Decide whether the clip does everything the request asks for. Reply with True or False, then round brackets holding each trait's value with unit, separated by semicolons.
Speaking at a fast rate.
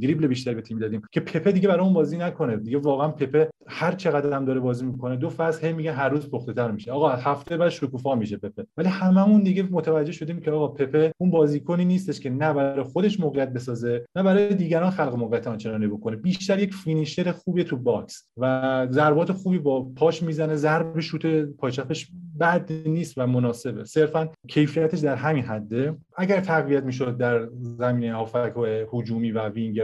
True (185 wpm)